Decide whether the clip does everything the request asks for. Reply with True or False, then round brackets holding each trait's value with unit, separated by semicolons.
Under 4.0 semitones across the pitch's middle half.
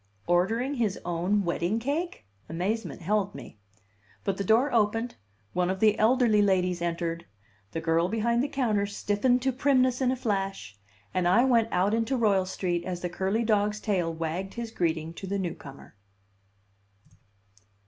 False (4.6 semitones)